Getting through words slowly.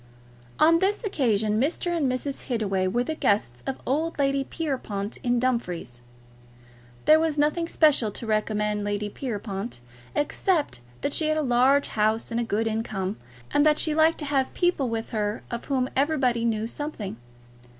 No: average, 165 wpm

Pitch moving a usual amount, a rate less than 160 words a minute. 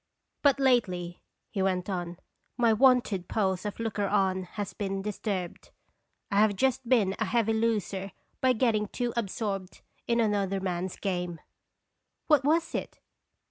Yes: average, 3.7 semitones; average, 140 wpm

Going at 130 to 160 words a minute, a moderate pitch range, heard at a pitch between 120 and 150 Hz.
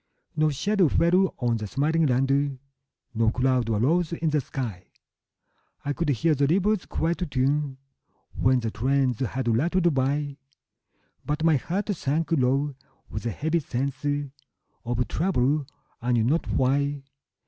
Yes: average, 140 wpm; average, 4.1 semitones; medium, 140 Hz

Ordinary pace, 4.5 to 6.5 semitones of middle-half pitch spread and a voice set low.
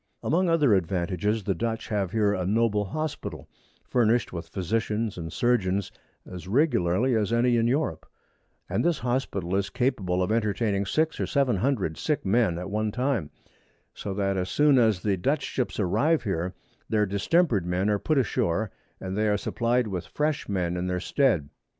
Yes: average, 170 wpm; average, 4.8 semitones; low, 105 Hz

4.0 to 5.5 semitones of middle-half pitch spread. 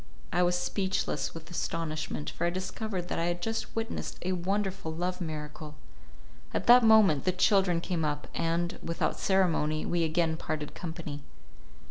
No: average, 2.7 semitones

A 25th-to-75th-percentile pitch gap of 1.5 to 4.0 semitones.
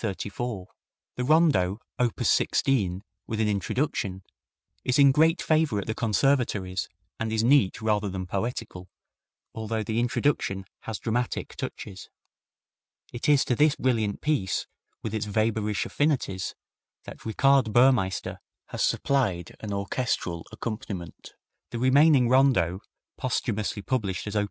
No: average, 4.7 semitones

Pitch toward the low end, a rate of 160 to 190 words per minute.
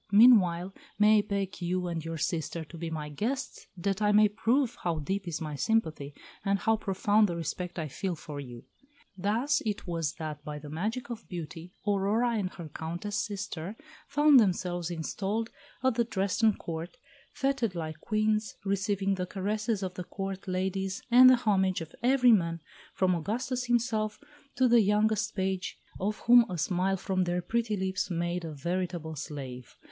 No: high, 190 Hz; average, 170 wpm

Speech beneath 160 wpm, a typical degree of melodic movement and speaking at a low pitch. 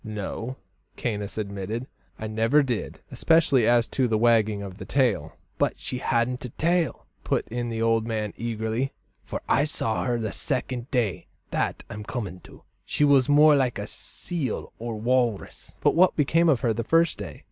No: average, 180 wpm; average, 3.6 semitones; low, 120 Hz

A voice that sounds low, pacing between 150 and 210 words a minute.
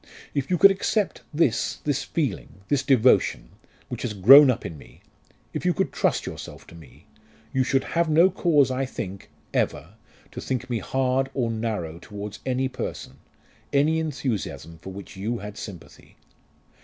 Yes: low, 125 Hz; average, 165 wpm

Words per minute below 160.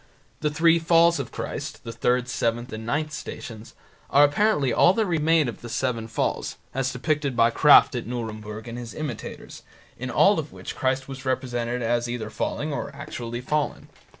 No: average, 175 wpm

